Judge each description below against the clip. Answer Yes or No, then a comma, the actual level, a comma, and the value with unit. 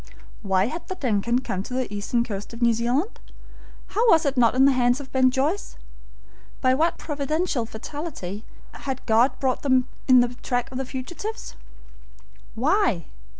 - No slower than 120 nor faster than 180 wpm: Yes, average, 165 wpm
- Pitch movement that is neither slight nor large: Yes, average, 3.7 semitones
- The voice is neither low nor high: No, very high, 255 Hz